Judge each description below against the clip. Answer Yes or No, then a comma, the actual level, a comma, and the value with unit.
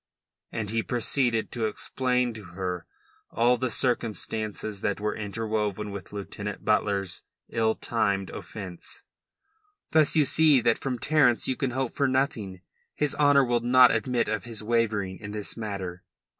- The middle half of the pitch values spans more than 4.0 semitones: No, average, 3.5 semitones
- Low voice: Yes, low, 110 Hz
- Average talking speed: Yes, average, 150 wpm